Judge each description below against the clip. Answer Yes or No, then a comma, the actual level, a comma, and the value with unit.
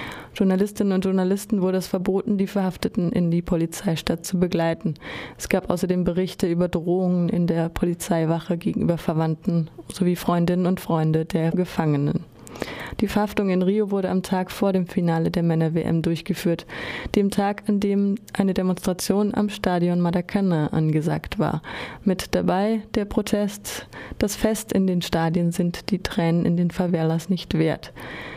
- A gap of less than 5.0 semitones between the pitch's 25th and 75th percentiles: Yes, average, 2.8 semitones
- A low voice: No, medium, 180 Hz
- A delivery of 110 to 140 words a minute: No, average, 150 wpm